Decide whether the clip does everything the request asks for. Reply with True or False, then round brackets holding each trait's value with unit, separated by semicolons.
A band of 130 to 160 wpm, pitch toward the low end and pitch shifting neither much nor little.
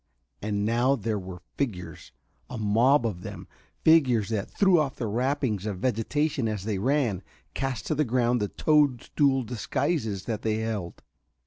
True (155 wpm; 115 Hz; 4.7 semitones)